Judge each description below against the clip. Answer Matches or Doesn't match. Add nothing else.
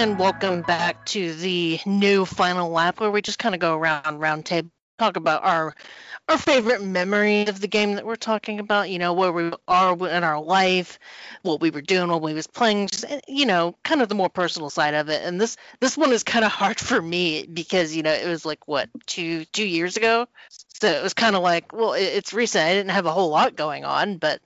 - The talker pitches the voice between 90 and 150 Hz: Doesn't match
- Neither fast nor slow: Doesn't match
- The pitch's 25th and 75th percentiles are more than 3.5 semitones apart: Matches